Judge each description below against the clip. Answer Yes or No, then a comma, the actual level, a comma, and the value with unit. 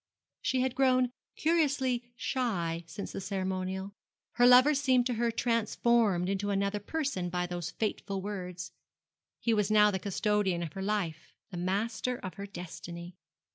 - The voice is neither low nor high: No, high, 205 Hz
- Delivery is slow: No, average, 150 wpm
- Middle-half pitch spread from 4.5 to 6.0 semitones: Yes, average, 4.8 semitones